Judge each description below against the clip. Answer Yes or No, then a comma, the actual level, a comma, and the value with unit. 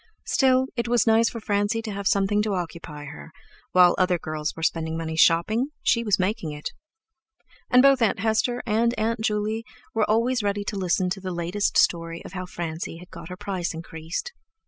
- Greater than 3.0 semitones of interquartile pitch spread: Yes, average, 4.7 semitones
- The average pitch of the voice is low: No, high, 200 Hz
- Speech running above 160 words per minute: Yes, average, 190 wpm